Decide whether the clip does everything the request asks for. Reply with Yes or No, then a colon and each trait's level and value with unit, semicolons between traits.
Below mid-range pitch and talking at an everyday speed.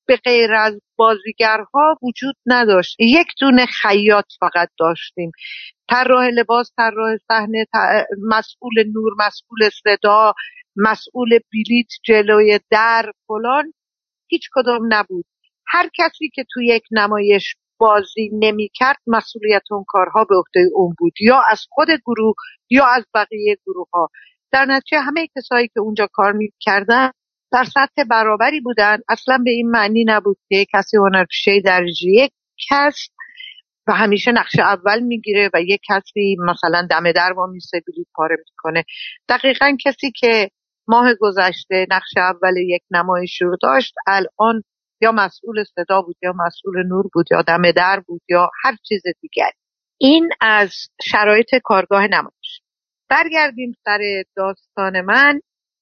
No: high, 215 Hz; average, 135 wpm